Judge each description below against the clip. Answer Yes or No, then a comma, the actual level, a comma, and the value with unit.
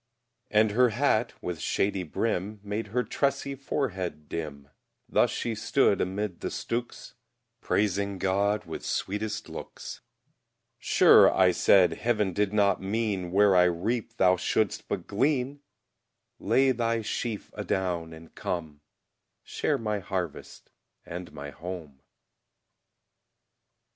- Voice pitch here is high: No, low, 100 Hz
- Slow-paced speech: Yes, slow, 120 wpm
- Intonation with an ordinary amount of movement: Yes, average, 3.9 semitones